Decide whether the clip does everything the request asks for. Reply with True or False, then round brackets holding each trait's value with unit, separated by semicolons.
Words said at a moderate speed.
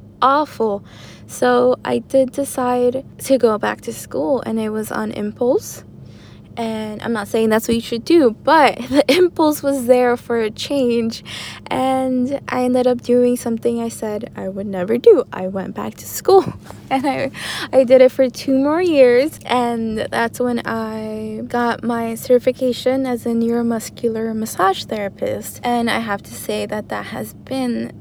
True (170 wpm)